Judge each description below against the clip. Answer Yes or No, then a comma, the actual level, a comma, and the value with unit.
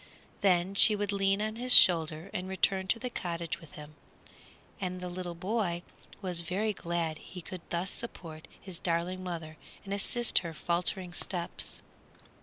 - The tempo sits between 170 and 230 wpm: No, average, 155 wpm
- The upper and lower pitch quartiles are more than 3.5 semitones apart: No, narrow, 2.6 semitones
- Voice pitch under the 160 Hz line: No, medium, 180 Hz